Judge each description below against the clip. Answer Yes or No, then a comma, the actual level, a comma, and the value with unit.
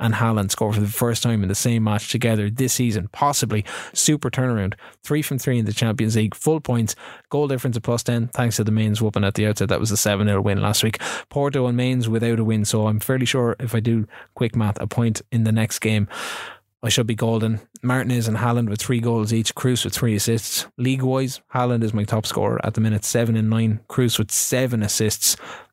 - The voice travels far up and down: No, narrow, 2.4 semitones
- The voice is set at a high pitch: No, low, 115 Hz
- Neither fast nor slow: No, fast, 235 wpm